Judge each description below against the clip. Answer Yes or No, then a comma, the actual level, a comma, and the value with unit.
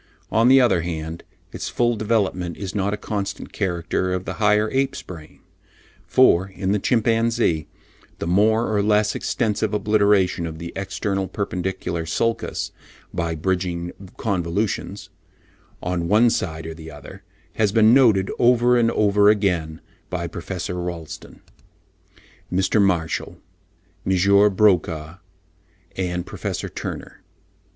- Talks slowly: Yes, slow, 125 wpm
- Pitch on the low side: Yes, very low, 95 Hz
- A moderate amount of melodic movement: Yes, average, 3.7 semitones